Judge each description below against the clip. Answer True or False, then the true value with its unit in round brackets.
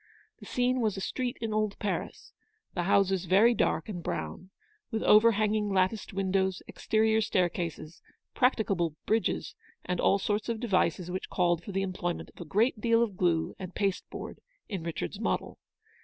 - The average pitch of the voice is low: False (195 Hz)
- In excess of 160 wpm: True (170 wpm)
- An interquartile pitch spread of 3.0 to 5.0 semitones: True (3.3 semitones)